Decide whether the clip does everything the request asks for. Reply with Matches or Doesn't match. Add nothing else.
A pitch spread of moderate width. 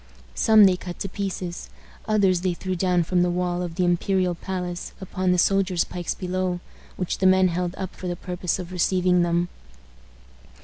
Doesn't match